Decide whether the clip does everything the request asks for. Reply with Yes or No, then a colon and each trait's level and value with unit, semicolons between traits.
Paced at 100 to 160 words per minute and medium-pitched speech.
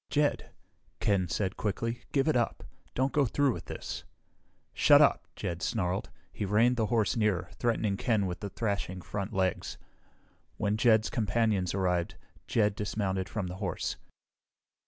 No: average, 150 wpm; low, 105 Hz